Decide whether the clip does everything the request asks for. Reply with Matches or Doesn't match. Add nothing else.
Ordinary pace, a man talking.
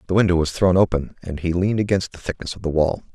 Doesn't match